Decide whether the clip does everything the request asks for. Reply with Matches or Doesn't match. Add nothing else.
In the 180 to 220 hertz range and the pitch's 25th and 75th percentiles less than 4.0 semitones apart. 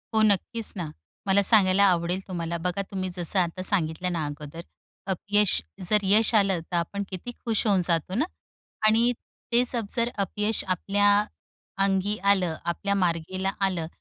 Matches